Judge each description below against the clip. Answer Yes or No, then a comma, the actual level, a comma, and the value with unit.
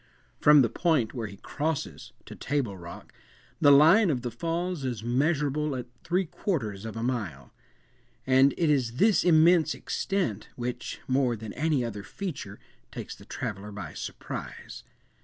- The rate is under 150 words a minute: No, average, 155 wpm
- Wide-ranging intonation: Yes, wide, 6.0 semitones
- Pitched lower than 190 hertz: Yes, low, 135 Hz